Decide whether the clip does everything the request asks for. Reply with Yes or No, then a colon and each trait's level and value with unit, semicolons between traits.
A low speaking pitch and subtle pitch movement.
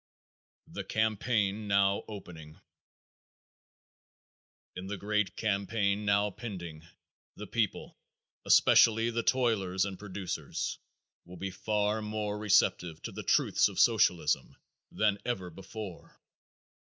Yes: low, 100 Hz; narrow, 2.3 semitones